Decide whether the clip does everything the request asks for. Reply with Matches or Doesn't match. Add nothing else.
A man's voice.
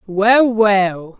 Doesn't match